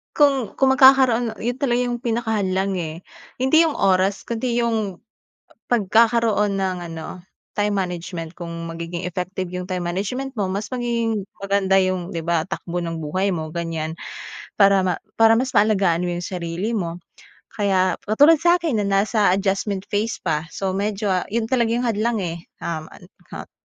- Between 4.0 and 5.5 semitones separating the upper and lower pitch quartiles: Yes, average, 4.3 semitones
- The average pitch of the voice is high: Yes, high, 195 Hz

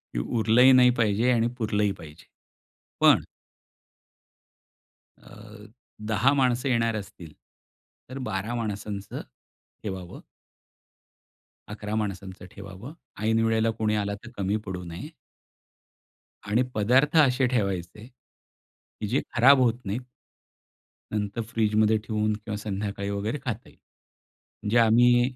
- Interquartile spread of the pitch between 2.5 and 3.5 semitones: Yes, average, 3.1 semitones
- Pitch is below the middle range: Yes, low, 110 Hz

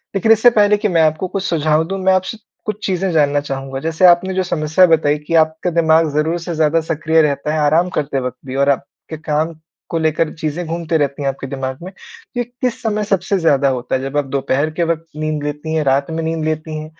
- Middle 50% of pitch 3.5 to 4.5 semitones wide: No, average, 3.1 semitones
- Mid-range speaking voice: Yes, medium, 160 Hz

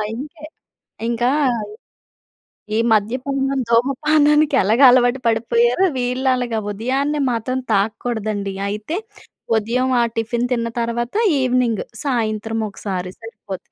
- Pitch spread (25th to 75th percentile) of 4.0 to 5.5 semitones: No, average, 2.8 semitones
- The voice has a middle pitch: No, high, 240 Hz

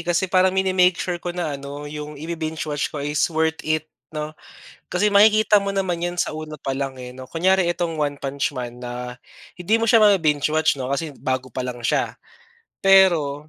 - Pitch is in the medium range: Yes, medium, 155 Hz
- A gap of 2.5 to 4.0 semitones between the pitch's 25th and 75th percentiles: No, average, 4.4 semitones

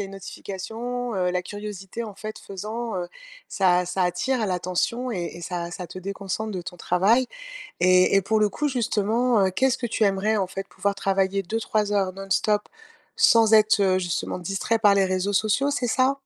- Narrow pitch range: No, average, 3.1 semitones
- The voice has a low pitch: No, high, 200 Hz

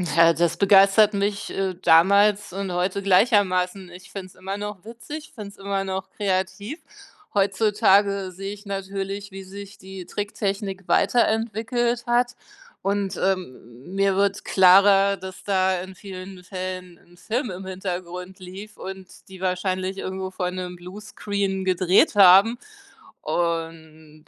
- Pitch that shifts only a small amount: Yes, narrow, 1.6 semitones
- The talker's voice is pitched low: No, high, 195 Hz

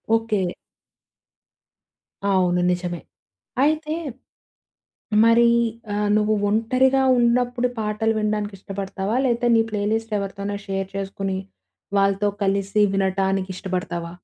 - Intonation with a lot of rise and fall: No, average, 2.7 semitones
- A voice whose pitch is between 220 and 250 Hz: No, high, 205 Hz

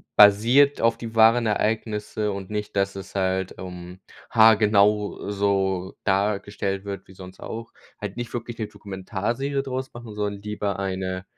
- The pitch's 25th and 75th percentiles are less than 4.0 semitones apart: Yes, narrow, 2.6 semitones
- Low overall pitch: Yes, low, 105 Hz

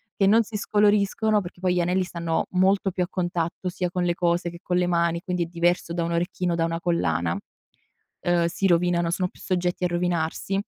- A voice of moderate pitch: Yes, medium, 175 Hz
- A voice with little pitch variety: Yes, narrow, 1.4 semitones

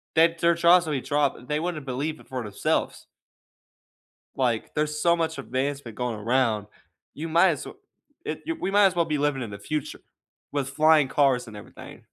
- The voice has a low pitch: No, medium, 145 Hz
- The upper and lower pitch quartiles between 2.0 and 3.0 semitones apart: No, average, 4.3 semitones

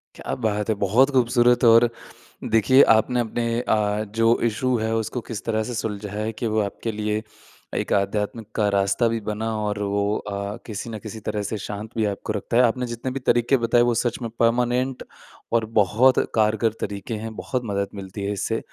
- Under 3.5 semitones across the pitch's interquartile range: Yes, narrow, 2.4 semitones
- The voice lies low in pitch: Yes, low, 110 Hz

